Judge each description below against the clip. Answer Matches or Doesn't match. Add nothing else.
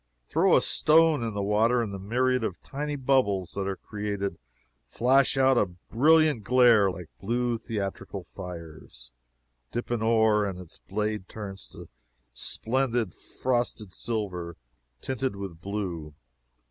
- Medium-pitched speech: Doesn't match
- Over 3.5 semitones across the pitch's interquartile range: Matches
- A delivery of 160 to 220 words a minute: Doesn't match